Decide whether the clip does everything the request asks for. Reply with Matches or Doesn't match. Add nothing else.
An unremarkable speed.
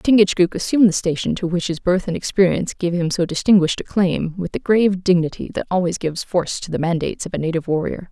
Doesn't match